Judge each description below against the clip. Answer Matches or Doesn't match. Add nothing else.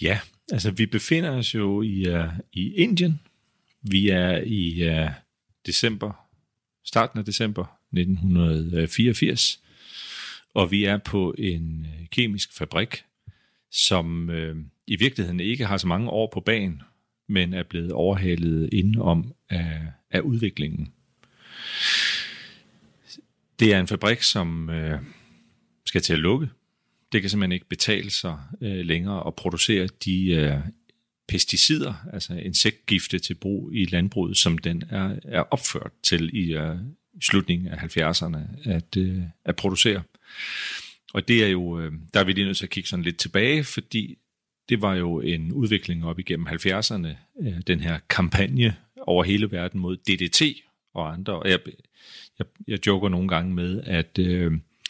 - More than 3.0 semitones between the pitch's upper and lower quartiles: Matches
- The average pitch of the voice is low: Matches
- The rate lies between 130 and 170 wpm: Matches